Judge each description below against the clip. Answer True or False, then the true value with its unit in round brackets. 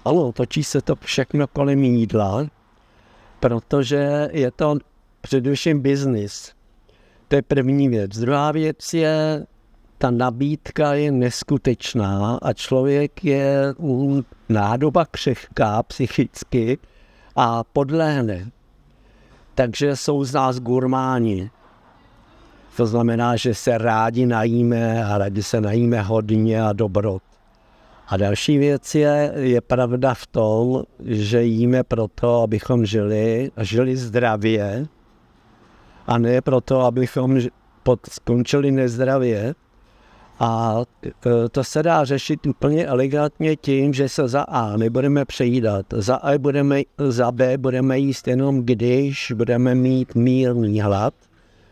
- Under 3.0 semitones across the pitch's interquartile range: False (3.6 semitones)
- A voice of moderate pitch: False (125 Hz)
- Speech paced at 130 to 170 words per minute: False (115 wpm)